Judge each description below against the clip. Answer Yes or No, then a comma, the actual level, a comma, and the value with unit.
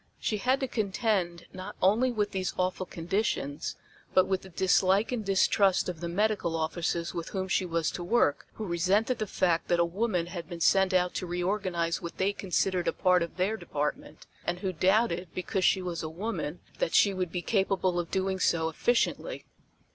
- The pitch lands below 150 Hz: No, medium, 185 Hz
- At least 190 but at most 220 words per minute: Yes, average, 195 wpm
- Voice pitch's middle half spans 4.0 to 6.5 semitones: No, average, 2.7 semitones